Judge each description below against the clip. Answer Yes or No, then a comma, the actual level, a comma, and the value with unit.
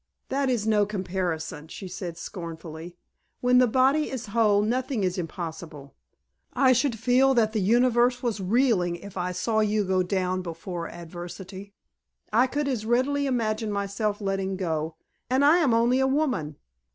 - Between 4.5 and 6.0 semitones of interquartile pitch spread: Yes, wide, 5.5 semitones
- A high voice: Yes, high, 210 Hz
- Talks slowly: No, average, 160 wpm